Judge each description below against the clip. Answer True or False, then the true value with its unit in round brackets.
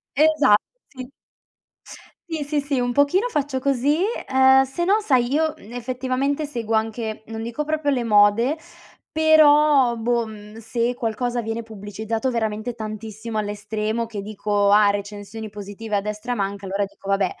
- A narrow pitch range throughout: False (4.1 semitones)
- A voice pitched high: True (230 Hz)